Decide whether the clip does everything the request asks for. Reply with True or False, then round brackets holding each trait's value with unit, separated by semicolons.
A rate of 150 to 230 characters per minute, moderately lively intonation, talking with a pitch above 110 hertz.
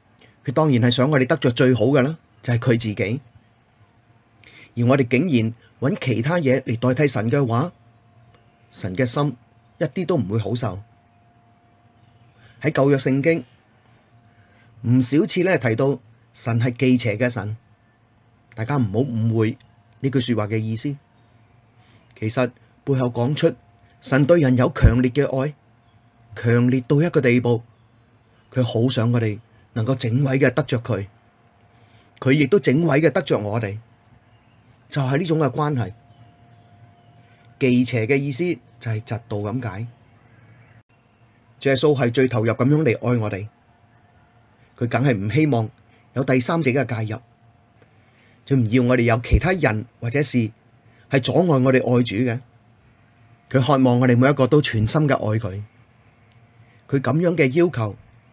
False (210 characters per minute; 2.2 semitones; 120 Hz)